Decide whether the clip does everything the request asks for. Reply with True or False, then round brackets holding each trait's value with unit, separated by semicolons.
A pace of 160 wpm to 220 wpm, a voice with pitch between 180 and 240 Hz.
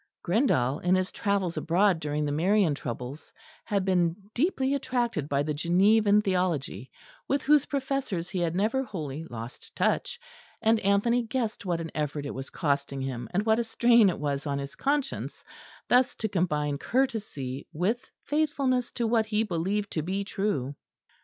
True (165 wpm; 190 Hz)